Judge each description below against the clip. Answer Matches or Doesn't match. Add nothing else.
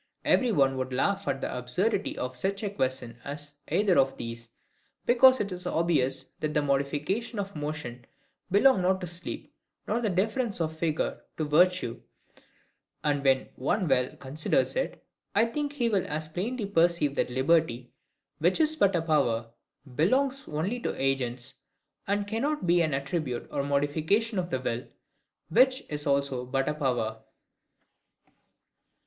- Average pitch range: Doesn't match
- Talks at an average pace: Matches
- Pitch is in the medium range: Matches